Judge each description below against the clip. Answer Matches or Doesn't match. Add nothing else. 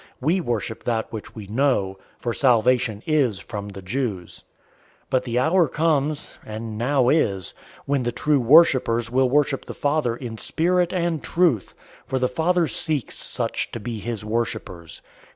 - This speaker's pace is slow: Doesn't match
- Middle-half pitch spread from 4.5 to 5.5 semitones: Matches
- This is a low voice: Matches